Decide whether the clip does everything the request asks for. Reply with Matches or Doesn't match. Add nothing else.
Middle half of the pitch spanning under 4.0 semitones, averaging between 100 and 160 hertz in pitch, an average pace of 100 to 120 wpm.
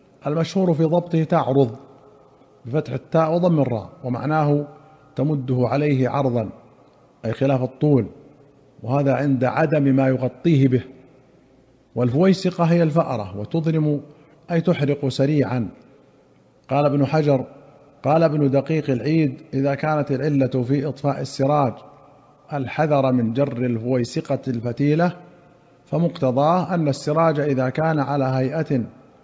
Matches